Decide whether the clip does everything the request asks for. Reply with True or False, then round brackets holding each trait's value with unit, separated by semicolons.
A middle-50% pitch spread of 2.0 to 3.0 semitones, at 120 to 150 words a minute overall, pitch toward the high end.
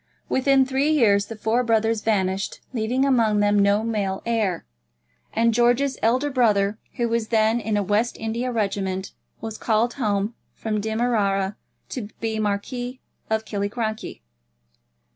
True (2.7 semitones; 140 wpm; 220 Hz)